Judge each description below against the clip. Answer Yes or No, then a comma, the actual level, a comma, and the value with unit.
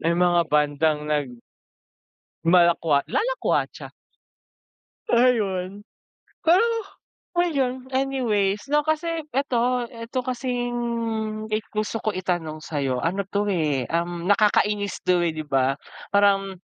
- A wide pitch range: Yes, wide, 6.2 semitones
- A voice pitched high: Yes, high, 205 Hz